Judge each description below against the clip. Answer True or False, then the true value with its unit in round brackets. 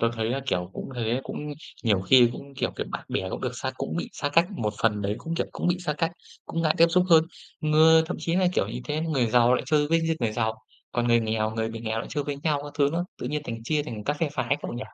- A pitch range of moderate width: False (5.8 semitones)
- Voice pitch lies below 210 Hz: True (140 Hz)